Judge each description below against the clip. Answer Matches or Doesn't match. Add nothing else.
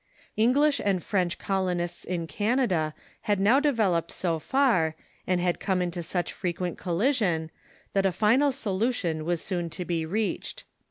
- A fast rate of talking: Doesn't match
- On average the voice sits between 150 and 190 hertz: Matches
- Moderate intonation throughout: Matches